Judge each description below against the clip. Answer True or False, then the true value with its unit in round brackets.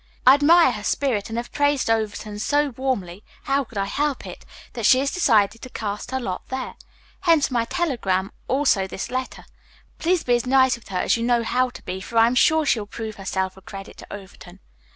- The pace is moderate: False (215 wpm)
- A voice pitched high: True (235 Hz)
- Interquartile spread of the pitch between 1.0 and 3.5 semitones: False (4.8 semitones)